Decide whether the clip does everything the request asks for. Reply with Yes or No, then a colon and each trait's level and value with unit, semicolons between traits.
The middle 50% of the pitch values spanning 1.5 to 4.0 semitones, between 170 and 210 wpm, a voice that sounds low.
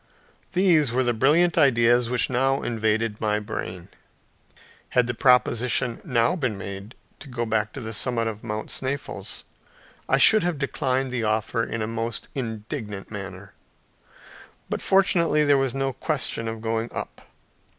No: average, 3.5 semitones; average, 150 wpm; low, 120 Hz